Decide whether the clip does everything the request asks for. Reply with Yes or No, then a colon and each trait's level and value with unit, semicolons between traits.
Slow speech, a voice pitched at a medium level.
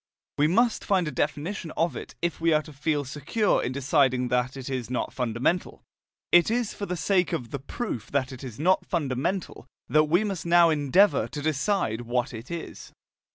No: average, 195 wpm; medium, 150 Hz